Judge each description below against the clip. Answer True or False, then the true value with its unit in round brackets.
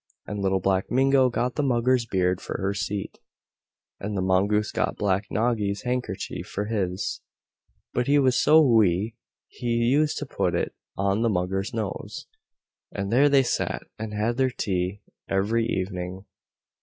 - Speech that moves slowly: False (155 wpm)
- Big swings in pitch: False (4.1 semitones)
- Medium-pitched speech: False (105 Hz)